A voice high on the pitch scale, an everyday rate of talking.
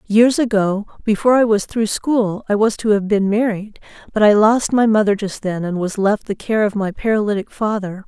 No: high, 210 Hz; fast, 215 wpm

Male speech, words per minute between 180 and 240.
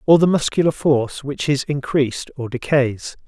No: male; average, 165 wpm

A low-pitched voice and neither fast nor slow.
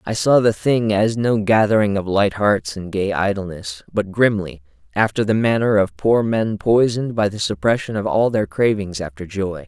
Yes: low, 105 Hz; average, 185 wpm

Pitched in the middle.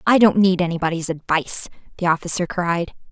Yes: medium, 175 Hz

